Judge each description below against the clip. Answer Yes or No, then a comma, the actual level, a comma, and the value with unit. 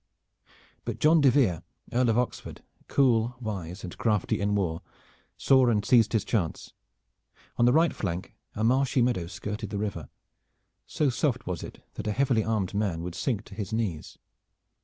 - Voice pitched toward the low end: Yes, low, 110 Hz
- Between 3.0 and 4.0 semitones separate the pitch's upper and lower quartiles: No, average, 4.5 semitones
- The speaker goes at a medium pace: Yes, average, 170 wpm